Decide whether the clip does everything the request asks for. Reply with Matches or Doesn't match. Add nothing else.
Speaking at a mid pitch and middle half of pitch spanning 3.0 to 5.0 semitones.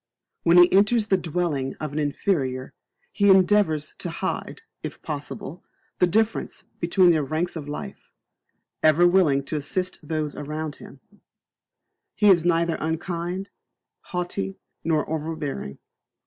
Matches